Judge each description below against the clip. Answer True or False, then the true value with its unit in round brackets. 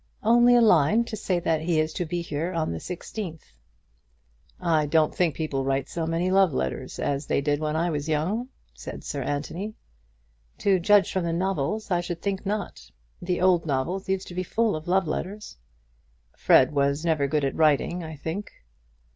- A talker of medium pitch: True (170 Hz)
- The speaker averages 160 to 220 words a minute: True (190 wpm)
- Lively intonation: False (4.0 semitones)